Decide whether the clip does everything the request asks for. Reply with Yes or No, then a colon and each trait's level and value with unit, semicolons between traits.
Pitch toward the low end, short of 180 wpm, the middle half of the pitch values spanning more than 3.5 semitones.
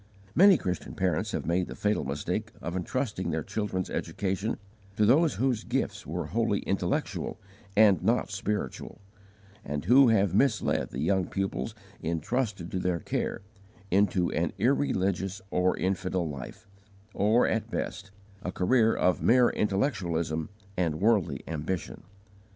Yes: very low, 95 Hz; slow, 135 wpm; average, 3.9 semitones